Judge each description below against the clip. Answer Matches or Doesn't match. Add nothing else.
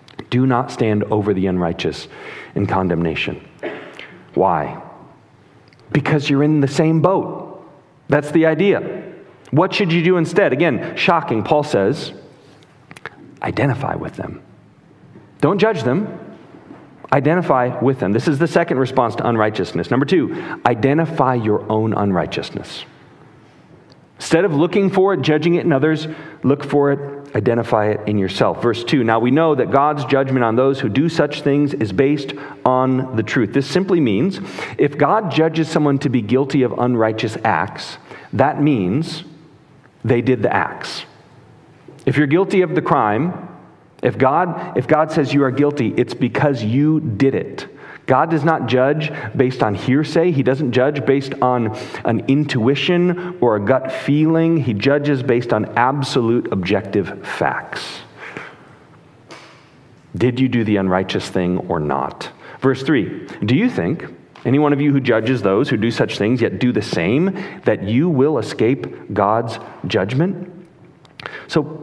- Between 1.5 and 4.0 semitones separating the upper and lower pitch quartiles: Doesn't match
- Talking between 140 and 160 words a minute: Matches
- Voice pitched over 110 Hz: Matches